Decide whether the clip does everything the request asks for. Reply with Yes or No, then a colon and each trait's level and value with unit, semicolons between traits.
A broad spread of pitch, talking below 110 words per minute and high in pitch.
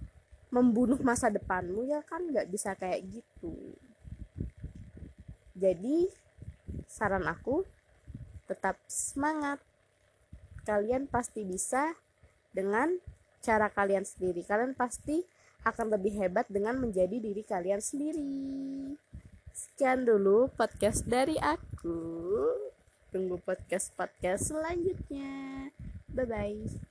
Yes: wide, 5.9 semitones; average, 90 wpm; high, 235 Hz